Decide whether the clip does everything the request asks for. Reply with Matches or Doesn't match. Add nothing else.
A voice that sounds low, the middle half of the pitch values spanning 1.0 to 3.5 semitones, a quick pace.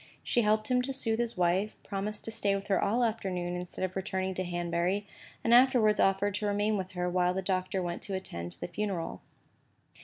Doesn't match